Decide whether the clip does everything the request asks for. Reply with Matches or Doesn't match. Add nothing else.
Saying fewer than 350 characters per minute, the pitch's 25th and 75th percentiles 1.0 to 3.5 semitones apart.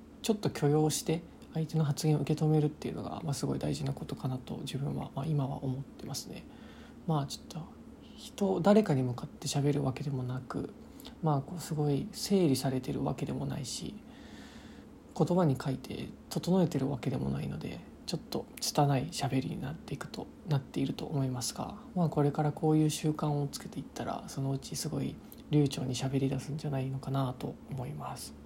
Matches